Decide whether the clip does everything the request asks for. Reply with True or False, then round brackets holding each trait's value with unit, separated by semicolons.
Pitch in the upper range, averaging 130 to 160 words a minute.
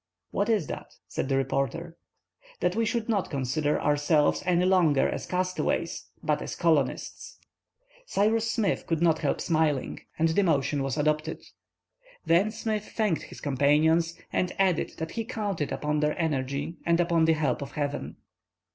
False (160 Hz; 155 wpm)